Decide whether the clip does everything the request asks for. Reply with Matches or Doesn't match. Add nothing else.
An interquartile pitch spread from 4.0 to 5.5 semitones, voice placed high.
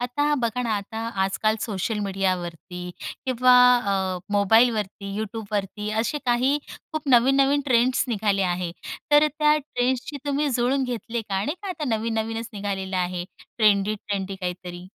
Matches